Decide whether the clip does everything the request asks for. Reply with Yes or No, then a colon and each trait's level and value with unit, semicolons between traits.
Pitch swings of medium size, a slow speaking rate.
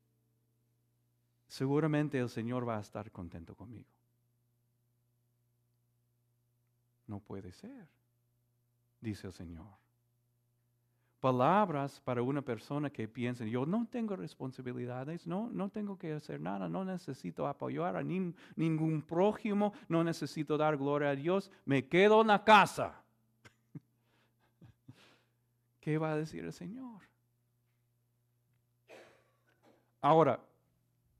Yes: average, 4.3 semitones; slow, 105 wpm